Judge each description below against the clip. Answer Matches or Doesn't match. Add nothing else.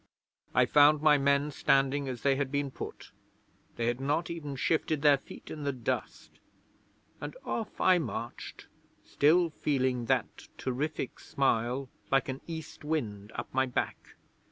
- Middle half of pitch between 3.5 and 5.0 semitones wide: Doesn't match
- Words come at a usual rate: Matches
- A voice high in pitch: Doesn't match